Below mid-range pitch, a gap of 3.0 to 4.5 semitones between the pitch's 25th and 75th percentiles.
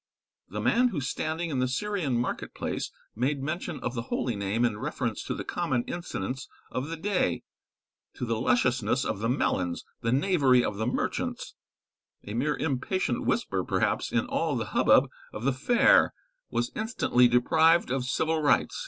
No: low, 130 Hz; average, 5.0 semitones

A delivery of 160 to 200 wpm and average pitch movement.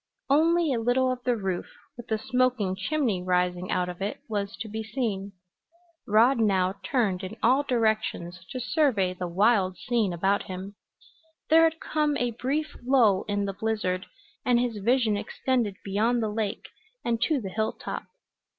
Yes: average, 165 wpm; average, 4.5 semitones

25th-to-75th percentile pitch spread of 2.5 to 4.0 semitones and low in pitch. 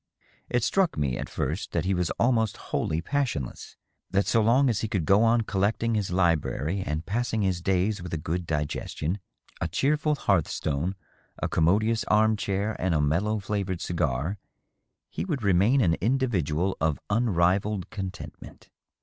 No: average, 4.7 semitones; very low, 95 Hz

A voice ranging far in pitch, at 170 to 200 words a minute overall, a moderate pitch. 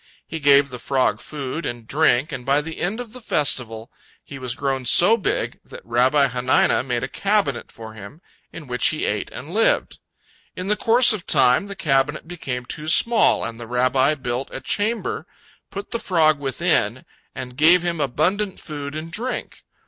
Yes: wide, 5.8 semitones; average, 180 wpm; medium, 145 Hz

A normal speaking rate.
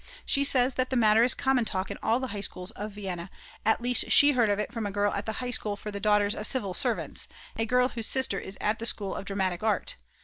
No: fast, 265 wpm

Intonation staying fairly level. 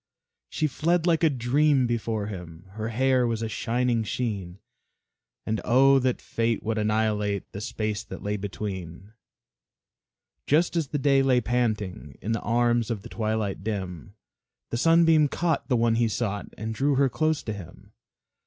No: average, 4.2 semitones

